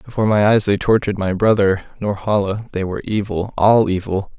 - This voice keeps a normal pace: Yes, average, 165 wpm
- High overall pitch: No, low, 100 Hz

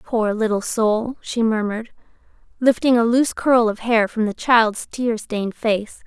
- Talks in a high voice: Yes, high, 225 Hz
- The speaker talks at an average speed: Yes, average, 170 wpm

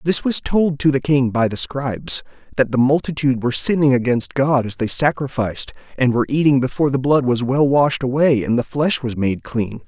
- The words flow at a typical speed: No, fast, 215 wpm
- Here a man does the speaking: Yes, male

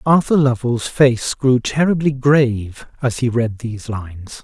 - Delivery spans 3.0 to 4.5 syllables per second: Yes, 4.3 syllables/s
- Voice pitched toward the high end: No, low, 125 Hz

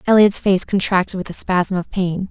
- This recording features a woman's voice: Yes, female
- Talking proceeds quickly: Yes, fast, 210 wpm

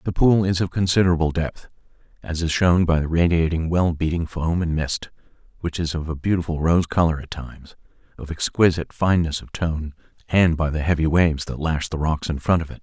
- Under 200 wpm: No, fast, 205 wpm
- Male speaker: Yes, male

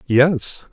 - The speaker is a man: Yes, male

